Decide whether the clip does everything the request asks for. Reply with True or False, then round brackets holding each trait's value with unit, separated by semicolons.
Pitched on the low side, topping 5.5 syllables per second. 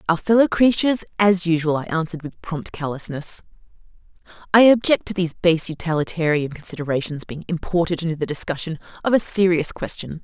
False (170 Hz; 6.0 syllables/s)